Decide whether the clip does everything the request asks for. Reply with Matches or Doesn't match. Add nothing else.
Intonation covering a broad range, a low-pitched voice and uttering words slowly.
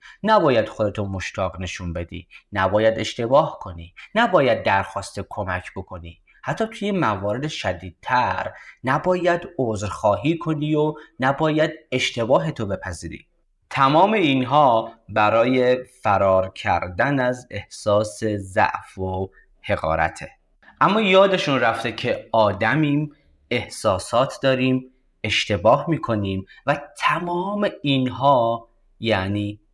Matches